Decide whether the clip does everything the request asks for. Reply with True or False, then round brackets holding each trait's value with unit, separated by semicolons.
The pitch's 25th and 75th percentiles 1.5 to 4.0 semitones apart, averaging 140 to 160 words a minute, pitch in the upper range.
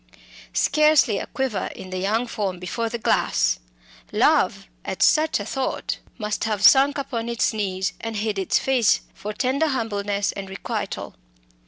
False (4.4 semitones; 155 wpm; 220 Hz)